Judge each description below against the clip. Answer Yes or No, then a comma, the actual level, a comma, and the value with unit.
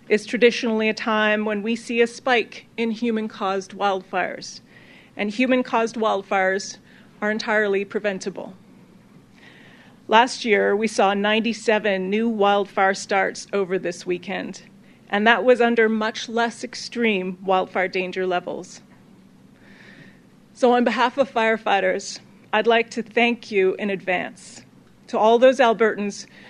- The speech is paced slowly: Yes, slow, 130 wpm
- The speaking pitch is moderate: No, high, 215 Hz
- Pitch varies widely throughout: No, average, 2.7 semitones